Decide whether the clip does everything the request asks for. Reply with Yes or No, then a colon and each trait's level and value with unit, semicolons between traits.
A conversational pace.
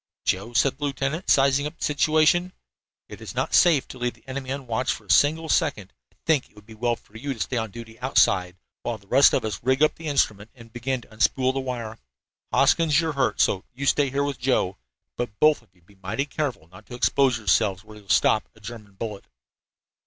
No: fast, 225 wpm